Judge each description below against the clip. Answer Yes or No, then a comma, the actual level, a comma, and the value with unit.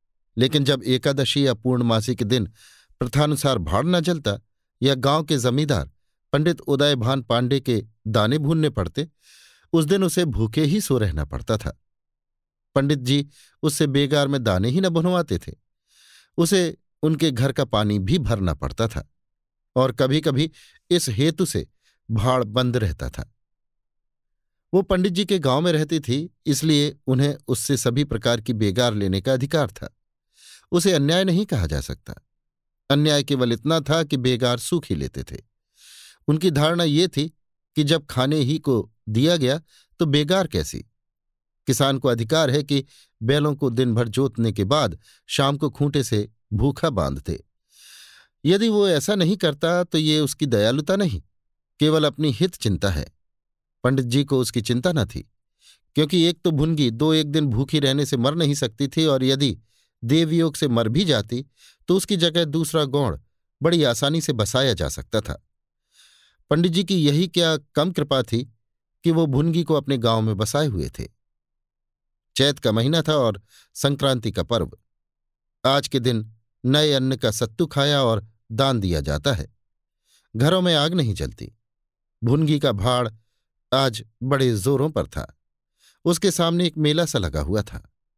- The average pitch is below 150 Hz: Yes, low, 135 Hz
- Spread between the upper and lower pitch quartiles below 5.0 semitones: No, average, 5.3 semitones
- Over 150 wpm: Yes, average, 165 wpm